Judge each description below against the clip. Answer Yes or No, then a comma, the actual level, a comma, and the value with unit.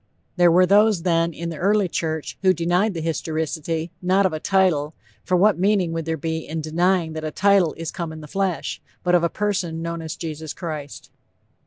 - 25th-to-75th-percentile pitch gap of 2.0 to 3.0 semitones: Yes, narrow, 2.6 semitones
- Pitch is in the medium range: Yes, medium, 170 Hz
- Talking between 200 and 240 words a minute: Yes, fast, 205 wpm